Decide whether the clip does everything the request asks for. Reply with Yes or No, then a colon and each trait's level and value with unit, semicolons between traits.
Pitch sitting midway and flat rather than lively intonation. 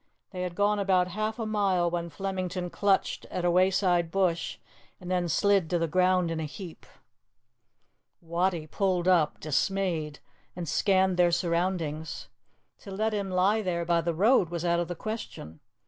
Yes: medium, 180 Hz; narrow, 2.2 semitones